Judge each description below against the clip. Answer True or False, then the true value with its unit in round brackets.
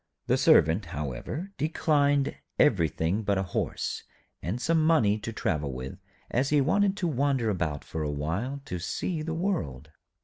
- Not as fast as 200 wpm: True (160 wpm)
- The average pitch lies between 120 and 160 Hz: False (110 Hz)